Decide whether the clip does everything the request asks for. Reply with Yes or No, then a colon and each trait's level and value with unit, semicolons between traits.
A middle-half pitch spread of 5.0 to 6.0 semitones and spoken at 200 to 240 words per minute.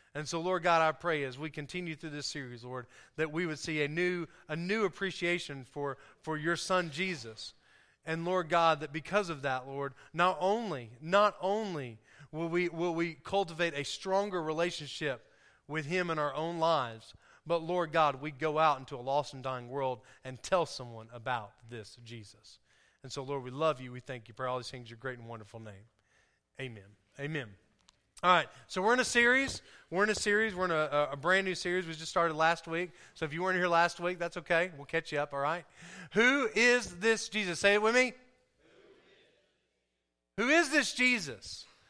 Yes: average, 5.3 semitones; fast, 205 wpm